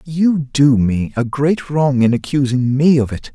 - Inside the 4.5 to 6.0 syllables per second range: No, 4.0 syllables/s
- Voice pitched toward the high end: No, low, 135 Hz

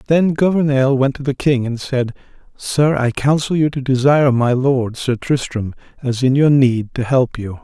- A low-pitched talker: Yes, low, 130 Hz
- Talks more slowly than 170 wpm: No, average, 195 wpm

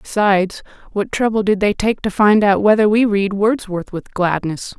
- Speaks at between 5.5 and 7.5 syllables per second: No, 4.7 syllables/s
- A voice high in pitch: Yes, high, 205 Hz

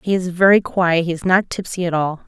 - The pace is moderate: No, fast, 235 wpm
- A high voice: No, medium, 180 Hz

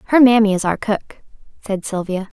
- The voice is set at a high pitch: Yes, high, 205 Hz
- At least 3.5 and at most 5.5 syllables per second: Yes, 5.4 syllables/s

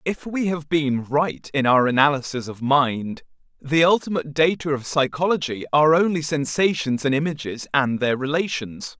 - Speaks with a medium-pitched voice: Yes, medium, 145 Hz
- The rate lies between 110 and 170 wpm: Yes, average, 155 wpm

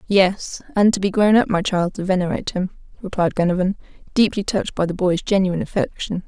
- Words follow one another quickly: No, average, 190 wpm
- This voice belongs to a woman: Yes, female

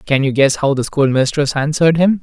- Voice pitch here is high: No, medium, 145 Hz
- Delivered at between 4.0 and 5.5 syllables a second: No, 5.7 syllables/s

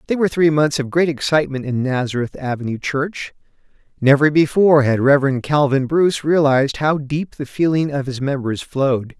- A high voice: No, medium, 140 Hz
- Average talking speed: Yes, average, 170 wpm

